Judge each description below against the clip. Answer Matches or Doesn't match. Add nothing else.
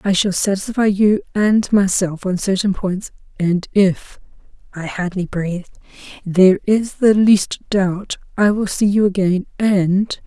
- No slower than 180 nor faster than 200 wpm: Doesn't match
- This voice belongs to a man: Doesn't match